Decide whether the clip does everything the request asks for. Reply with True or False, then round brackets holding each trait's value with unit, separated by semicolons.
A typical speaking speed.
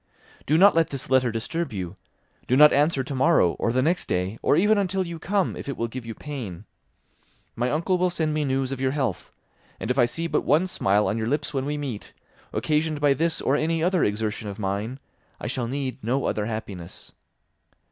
False (210 wpm)